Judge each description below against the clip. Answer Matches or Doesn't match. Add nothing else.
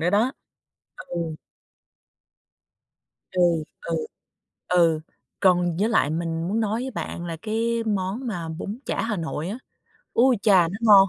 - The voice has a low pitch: Doesn't match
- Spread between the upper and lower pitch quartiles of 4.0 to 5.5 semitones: Matches